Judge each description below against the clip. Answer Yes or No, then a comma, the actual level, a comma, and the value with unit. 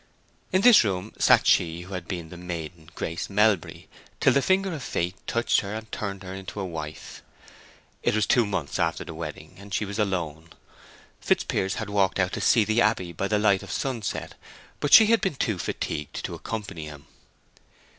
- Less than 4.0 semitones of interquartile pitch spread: No, average, 4.3 semitones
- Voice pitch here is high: No, very low, 95 Hz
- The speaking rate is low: No, average, 195 wpm